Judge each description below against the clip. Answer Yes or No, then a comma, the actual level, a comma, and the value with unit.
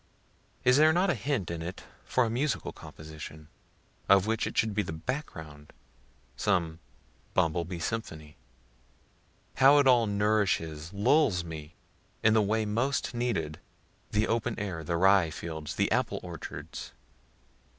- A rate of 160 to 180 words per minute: No, average, 145 wpm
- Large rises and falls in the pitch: Yes, wide, 6.4 semitones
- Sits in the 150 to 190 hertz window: No, low, 100 Hz